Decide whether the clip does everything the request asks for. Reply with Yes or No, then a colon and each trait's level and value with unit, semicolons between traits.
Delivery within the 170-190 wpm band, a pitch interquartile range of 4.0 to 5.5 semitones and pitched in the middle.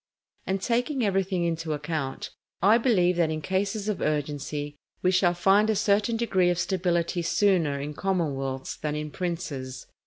No: average, 155 wpm; average, 4.5 semitones; medium, 175 Hz